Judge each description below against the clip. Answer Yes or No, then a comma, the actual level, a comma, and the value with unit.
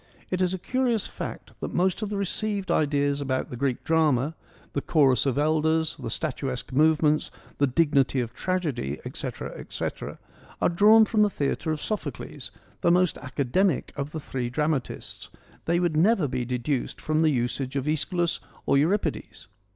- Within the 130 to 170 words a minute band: Yes, average, 165 wpm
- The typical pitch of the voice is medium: Yes, medium, 155 Hz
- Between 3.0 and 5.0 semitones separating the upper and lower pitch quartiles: Yes, average, 4.6 semitones